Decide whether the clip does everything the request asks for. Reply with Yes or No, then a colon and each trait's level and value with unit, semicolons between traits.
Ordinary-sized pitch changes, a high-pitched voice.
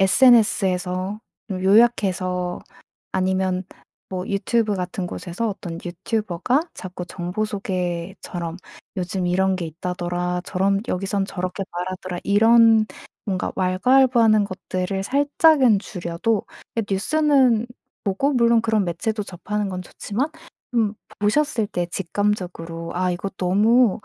Yes: average, 3.5 semitones; high, 195 Hz